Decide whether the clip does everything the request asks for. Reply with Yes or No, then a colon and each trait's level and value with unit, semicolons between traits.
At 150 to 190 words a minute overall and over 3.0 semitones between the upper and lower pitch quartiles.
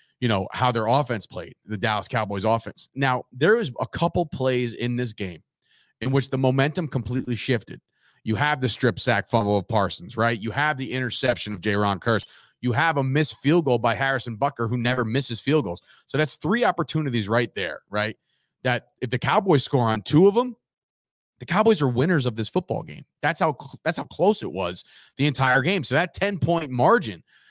No: fast, 205 wpm; average, 4.1 semitones